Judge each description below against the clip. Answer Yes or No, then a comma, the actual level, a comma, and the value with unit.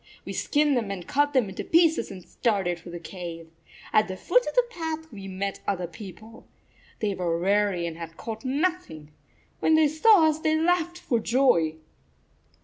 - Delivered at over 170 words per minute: Yes, average, 190 wpm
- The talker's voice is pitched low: No, high, 215 Hz